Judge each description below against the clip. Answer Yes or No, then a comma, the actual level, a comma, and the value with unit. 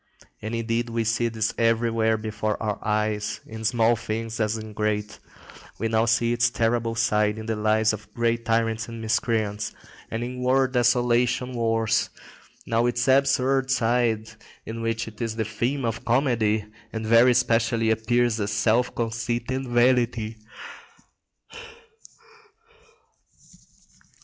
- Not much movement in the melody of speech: Yes, narrow, 1.5 semitones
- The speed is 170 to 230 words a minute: No, slow, 135 wpm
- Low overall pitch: Yes, low, 115 Hz